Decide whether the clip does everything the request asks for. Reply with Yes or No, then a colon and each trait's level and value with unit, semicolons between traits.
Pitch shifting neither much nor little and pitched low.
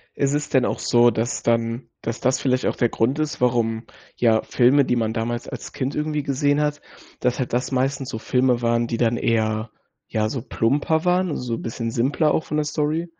Yes: average, 3.7 semitones; low, 125 Hz